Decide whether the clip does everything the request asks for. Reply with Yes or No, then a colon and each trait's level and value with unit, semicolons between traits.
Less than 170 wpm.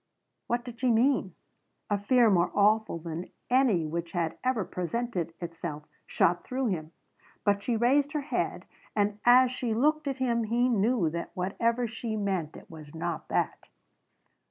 Yes: average, 160 wpm